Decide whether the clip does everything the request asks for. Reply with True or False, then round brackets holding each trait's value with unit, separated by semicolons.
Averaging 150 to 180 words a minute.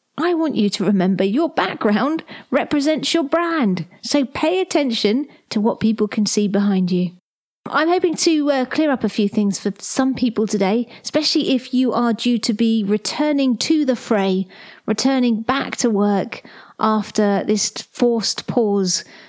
True (160 wpm)